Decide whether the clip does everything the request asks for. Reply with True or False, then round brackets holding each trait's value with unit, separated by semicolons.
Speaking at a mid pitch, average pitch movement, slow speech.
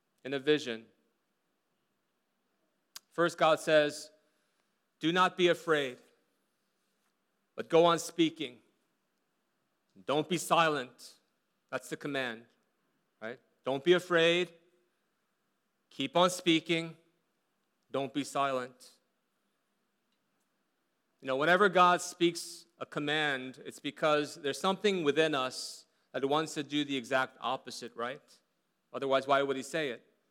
True (155 Hz; 3.8 semitones; 115 wpm)